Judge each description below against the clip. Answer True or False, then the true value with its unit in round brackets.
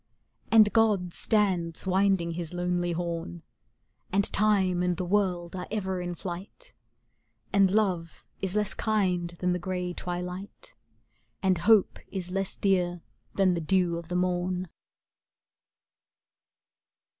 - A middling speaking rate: False (130 wpm)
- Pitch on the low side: False (180 Hz)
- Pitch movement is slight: True (1.9 semitones)